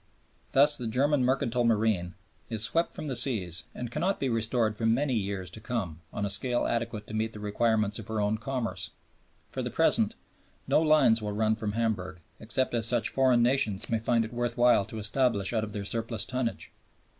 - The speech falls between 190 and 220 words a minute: Yes, average, 200 wpm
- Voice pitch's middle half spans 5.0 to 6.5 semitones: No, average, 2.8 semitones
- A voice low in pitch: Yes, low, 115 Hz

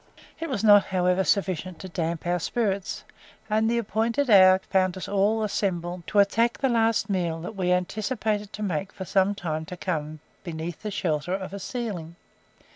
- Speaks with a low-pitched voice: No, high, 190 Hz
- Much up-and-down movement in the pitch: No, average, 3.2 semitones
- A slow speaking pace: No, average, 180 wpm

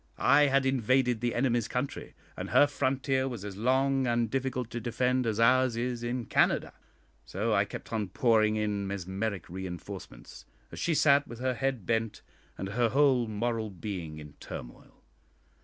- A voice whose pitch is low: Yes, low, 120 Hz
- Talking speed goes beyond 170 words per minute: No, average, 165 wpm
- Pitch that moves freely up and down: No, average, 3.8 semitones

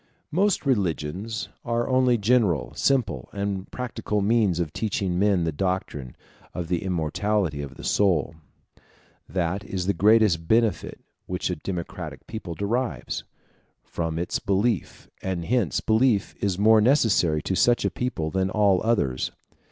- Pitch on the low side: Yes, low, 100 Hz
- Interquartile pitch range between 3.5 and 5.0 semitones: Yes, average, 4.7 semitones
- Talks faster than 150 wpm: No, average, 145 wpm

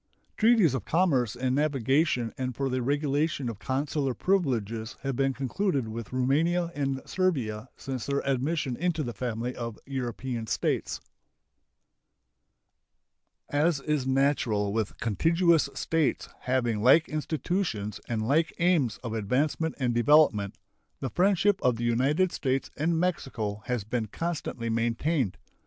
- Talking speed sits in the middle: No, slow, 130 wpm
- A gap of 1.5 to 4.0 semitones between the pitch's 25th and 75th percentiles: No, average, 4.9 semitones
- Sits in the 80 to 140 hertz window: Yes, low, 135 Hz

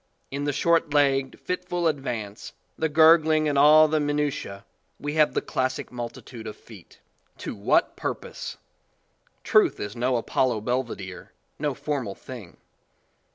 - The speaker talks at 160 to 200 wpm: No, average, 140 wpm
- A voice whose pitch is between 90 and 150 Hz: Yes, medium, 140 Hz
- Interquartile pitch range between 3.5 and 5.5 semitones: Yes, average, 4.2 semitones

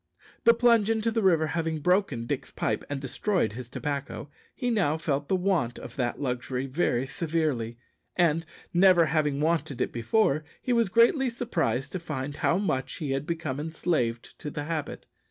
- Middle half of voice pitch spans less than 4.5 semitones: No, wide, 5.5 semitones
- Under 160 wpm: No, average, 175 wpm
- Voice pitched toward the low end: No, medium, 155 Hz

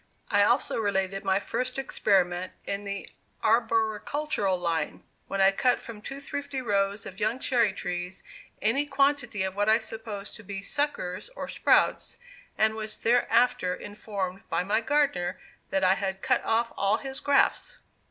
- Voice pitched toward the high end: Yes, high, 210 Hz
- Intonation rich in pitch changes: No, average, 4.2 semitones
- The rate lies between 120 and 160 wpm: Yes, average, 155 wpm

